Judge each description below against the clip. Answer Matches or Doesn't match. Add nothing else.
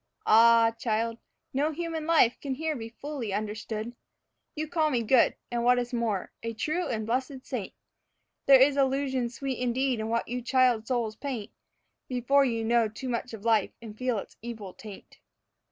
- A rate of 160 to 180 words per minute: Matches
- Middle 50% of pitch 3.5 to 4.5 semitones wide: Doesn't match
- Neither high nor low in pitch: Doesn't match